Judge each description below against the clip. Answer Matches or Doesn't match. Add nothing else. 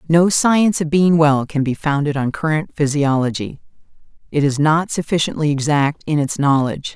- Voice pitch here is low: Doesn't match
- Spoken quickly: Doesn't match